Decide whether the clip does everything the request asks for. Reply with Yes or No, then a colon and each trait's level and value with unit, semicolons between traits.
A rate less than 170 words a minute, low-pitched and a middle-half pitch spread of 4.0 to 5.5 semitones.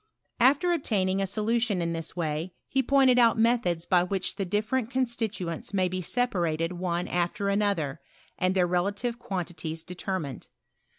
No: average, 155 wpm; high, 190 Hz; average, 4.9 semitones